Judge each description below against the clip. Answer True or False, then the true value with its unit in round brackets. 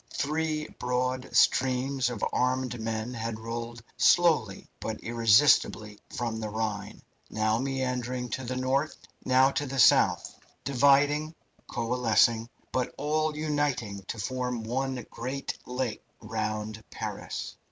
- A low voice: True (125 Hz)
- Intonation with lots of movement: False (3.2 semitones)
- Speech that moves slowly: True (120 wpm)